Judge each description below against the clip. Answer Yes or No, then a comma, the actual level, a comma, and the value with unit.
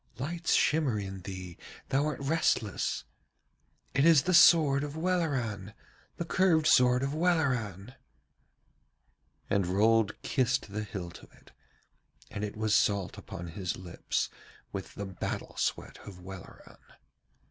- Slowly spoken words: Yes, slow, 130 wpm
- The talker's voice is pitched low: Yes, low, 115 Hz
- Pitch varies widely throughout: Yes, wide, 7.4 semitones